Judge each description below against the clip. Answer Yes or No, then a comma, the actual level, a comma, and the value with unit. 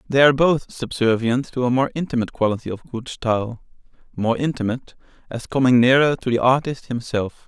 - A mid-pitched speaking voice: No, low, 125 Hz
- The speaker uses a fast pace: No, average, 170 wpm